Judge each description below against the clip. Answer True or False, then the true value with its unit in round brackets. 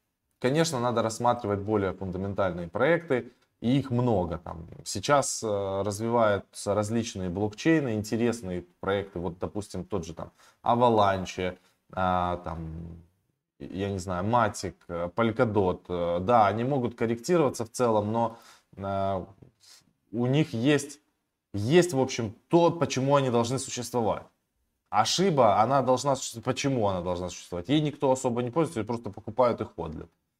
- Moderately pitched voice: False (110 Hz)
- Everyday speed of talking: True (125 wpm)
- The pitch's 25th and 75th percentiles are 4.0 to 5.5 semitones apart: True (5.1 semitones)